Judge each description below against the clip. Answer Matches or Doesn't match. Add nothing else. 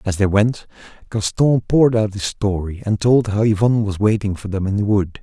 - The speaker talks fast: Matches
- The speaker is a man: Matches